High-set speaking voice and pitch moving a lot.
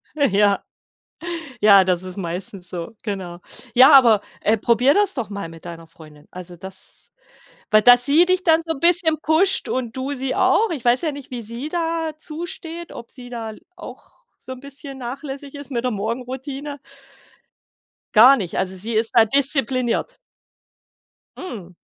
Yes: high, 245 Hz; wide, 6.0 semitones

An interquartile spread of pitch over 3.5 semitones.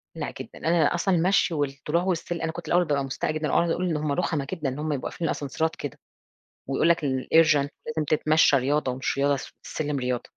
No: average, 2.9 semitones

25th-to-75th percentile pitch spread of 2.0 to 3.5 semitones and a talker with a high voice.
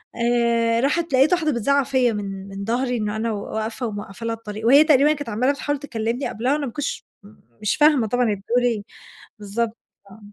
No: average, 4.1 semitones; high, 235 Hz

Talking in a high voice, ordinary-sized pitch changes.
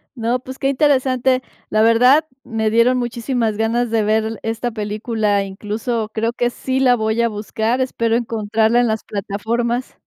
No: high, 230 Hz; narrow, 2.1 semitones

